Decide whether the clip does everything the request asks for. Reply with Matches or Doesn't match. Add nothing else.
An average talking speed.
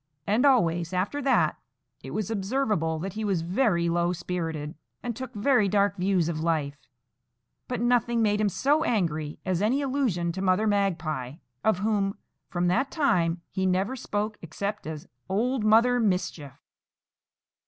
Matches